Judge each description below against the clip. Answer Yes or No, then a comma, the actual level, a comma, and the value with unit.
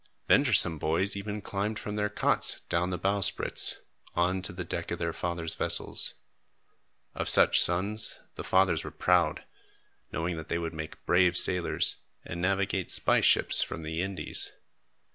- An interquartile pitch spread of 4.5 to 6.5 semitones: No, average, 2.7 semitones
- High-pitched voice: No, very low, 90 Hz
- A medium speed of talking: Yes, average, 155 wpm